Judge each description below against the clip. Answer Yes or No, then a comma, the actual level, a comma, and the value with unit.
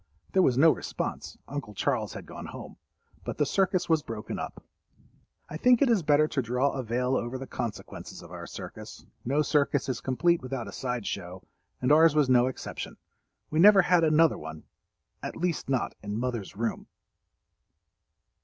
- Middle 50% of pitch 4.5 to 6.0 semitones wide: Yes, average, 4.9 semitones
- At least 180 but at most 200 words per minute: No, average, 165 wpm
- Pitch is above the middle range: No, low, 135 Hz